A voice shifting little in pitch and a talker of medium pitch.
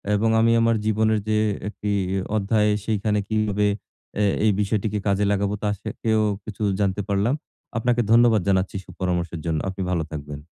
No: narrow, 2.1 semitones; low, 105 Hz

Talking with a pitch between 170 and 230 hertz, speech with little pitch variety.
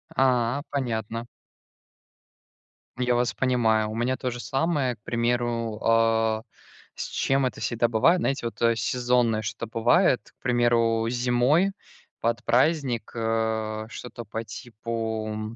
No: low, 120 Hz; narrow, 1.8 semitones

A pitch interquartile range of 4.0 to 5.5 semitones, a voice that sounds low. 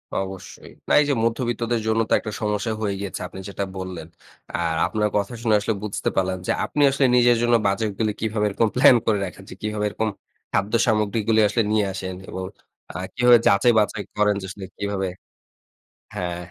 No: average, 2.7 semitones; low, 105 Hz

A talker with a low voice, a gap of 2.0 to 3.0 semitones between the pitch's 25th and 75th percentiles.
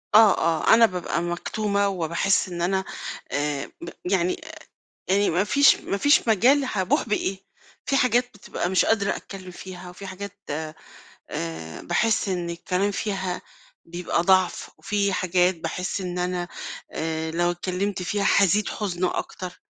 No: medium, 185 Hz; narrow, 2.5 semitones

